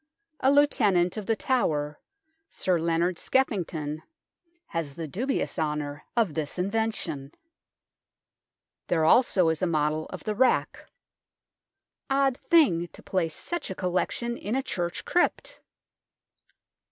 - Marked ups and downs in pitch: Yes, wide, 6.9 semitones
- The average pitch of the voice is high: No, medium, 180 Hz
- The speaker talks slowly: Yes, slow, 120 wpm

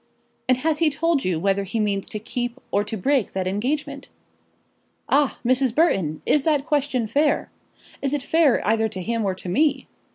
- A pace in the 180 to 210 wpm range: Yes, average, 185 wpm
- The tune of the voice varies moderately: No, wide, 6.2 semitones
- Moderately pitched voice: No, very high, 250 Hz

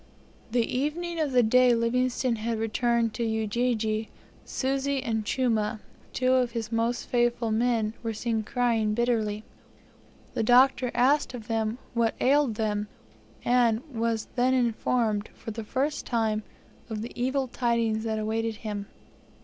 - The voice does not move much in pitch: Yes, narrow, 2.2 semitones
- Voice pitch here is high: Yes, high, 230 Hz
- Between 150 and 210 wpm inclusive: No, average, 140 wpm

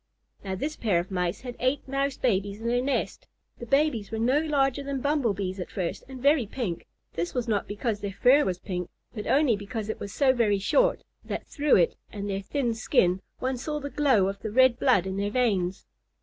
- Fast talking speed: Yes, fast, 220 wpm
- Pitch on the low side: No, high, 230 Hz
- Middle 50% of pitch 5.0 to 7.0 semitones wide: Yes, wide, 5.4 semitones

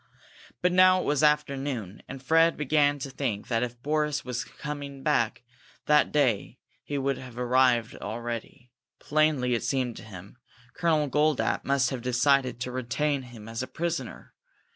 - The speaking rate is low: No, average, 165 wpm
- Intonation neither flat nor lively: Yes, average, 3.5 semitones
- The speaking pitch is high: No, low, 135 Hz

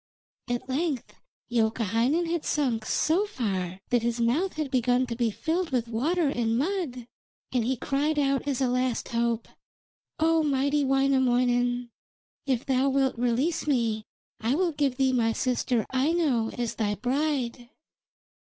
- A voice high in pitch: Yes, very high, 255 Hz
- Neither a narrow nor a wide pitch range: Yes, average, 3.4 semitones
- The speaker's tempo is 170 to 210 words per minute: No, average, 145 wpm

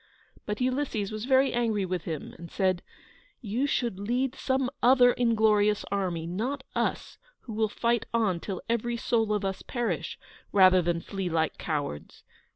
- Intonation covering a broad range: No, average, 4.5 semitones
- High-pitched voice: Yes, high, 215 Hz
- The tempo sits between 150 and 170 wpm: Yes, average, 160 wpm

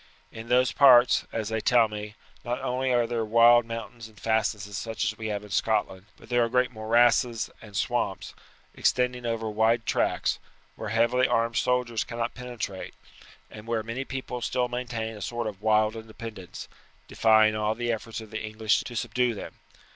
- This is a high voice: No, low, 115 Hz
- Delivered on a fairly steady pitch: Yes, narrow, 1.8 semitones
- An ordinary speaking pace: Yes, average, 175 wpm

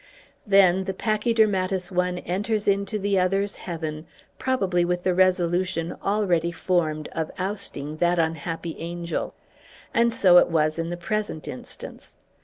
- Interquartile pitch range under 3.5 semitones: Yes, average, 2.8 semitones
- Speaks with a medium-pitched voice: Yes, medium, 180 Hz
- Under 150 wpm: Yes, slow, 135 wpm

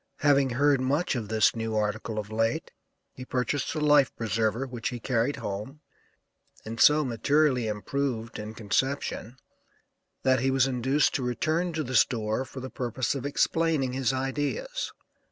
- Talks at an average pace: Yes, average, 155 wpm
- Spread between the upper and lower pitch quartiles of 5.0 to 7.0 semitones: No, average, 3.8 semitones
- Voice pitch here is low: Yes, low, 130 Hz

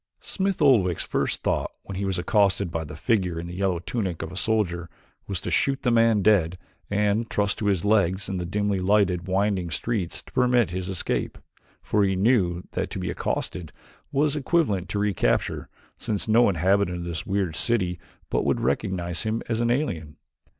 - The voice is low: Yes, very low, 95 Hz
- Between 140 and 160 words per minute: No, average, 185 wpm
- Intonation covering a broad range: No, average, 3.7 semitones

